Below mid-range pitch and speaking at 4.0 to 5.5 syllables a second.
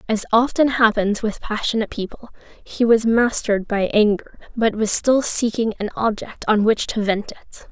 No: high, 220 Hz; 4.9 syllables/s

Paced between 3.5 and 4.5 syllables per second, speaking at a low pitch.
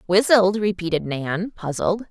No: 4.2 syllables/s; high, 190 Hz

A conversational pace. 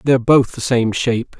No: fast, 215 wpm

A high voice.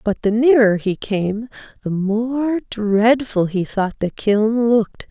Yes: high, 220 Hz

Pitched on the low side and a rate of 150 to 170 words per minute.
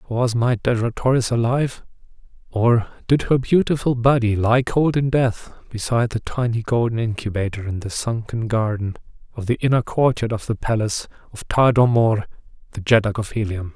Yes: low, 115 Hz; average, 160 wpm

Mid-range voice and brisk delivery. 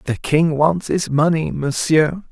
No: medium, 155 Hz; average, 155 wpm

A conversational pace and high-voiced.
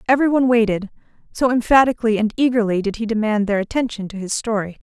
Yes: average, 170 wpm; high, 225 Hz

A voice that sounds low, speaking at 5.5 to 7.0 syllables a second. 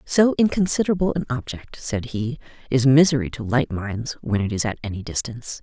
Yes: low, 130 Hz; 5.6 syllables/s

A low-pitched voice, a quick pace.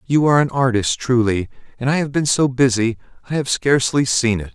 Yes: low, 125 Hz; fast, 210 wpm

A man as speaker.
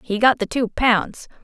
No: female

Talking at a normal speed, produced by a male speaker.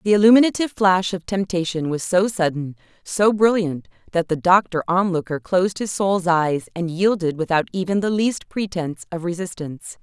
No: average, 160 wpm; female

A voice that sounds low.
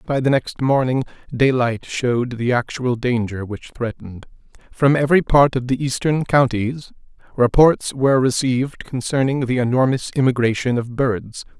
Yes: low, 125 Hz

